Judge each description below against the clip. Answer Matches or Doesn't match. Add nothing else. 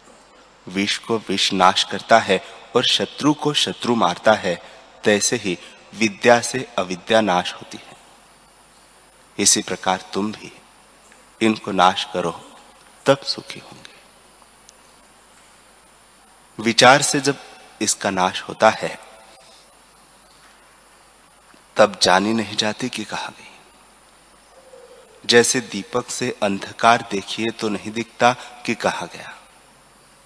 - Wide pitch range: Doesn't match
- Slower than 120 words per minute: Matches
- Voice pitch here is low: Matches